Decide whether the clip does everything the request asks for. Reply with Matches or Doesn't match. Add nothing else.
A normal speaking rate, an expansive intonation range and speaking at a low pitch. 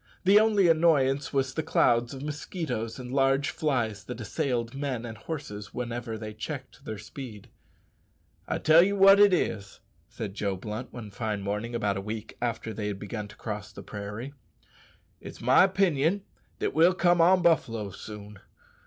Matches